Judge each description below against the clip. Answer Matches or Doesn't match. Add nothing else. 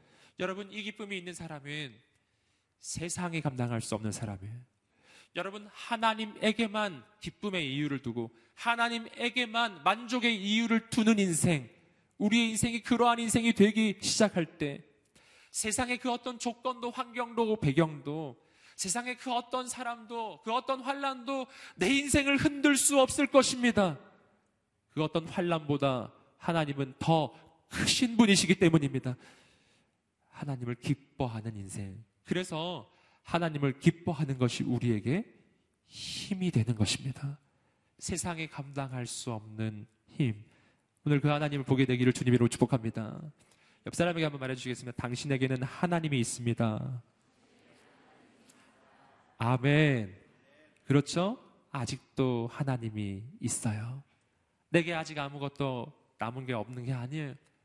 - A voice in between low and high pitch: Matches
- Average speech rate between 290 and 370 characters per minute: Doesn't match